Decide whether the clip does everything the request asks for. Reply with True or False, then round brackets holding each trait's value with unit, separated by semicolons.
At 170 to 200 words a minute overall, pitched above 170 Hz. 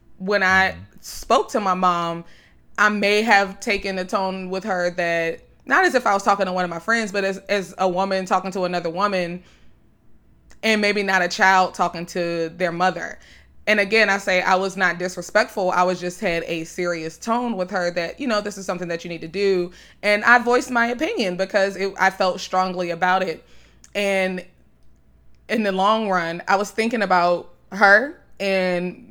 True (195 wpm; 190 Hz)